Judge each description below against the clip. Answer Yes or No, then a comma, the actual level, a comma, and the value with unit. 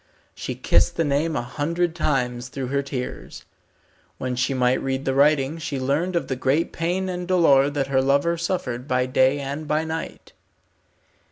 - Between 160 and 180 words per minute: Yes, average, 175 wpm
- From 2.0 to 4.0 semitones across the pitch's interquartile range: Yes, average, 3.7 semitones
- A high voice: No, medium, 140 Hz